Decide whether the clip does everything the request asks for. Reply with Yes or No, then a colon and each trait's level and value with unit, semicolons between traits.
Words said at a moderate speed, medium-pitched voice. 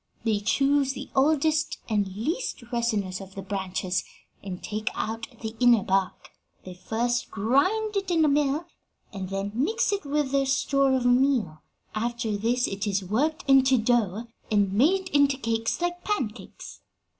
No: average, 155 wpm; high, 240 Hz